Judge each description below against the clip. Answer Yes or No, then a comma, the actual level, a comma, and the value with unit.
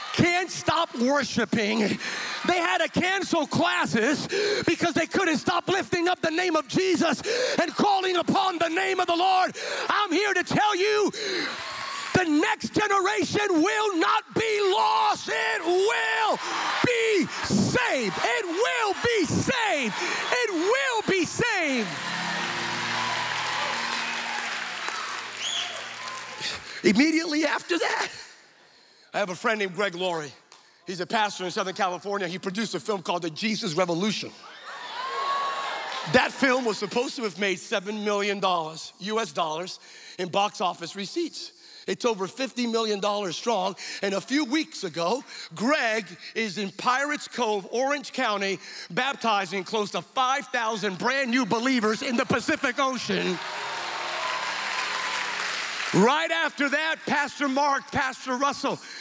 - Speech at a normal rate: No, slow, 125 wpm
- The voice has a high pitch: Yes, very high, 275 Hz